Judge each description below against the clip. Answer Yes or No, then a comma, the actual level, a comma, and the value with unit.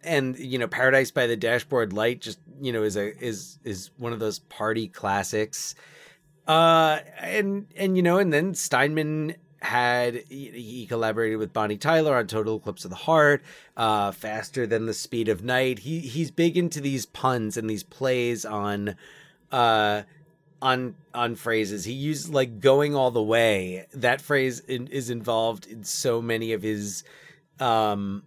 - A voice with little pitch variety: No, average, 5.0 semitones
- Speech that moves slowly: No, average, 170 wpm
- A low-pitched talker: Yes, low, 120 Hz